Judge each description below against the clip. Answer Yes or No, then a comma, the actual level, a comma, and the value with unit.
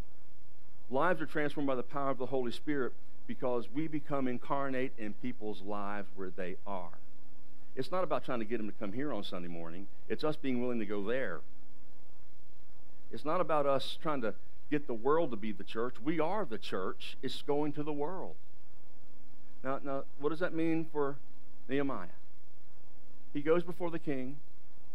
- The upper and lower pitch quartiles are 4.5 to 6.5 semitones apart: No, average, 3.7 semitones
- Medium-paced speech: Yes, average, 180 wpm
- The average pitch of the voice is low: Yes, low, 130 Hz